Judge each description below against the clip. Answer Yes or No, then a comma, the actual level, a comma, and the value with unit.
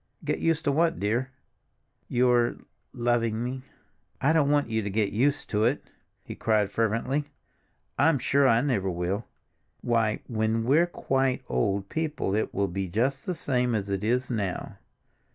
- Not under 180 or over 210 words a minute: No, average, 155 wpm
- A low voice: Yes, low, 120 Hz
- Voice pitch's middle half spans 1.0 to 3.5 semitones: No, average, 4.4 semitones